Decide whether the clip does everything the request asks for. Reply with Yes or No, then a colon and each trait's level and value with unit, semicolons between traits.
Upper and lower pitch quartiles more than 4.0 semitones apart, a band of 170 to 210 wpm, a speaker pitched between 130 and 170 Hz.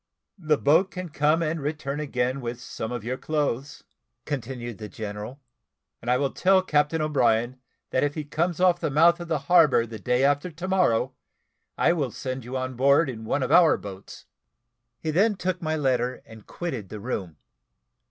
Yes: average, 4.7 semitones; average, 185 wpm; medium, 140 Hz